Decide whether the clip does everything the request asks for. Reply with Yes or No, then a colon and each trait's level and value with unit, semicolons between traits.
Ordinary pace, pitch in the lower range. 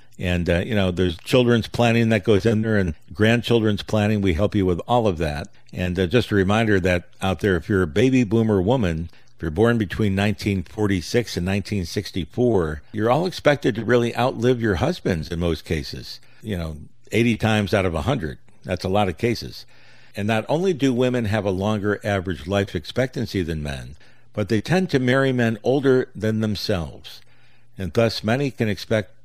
Yes: average, 190 wpm; low, 105 Hz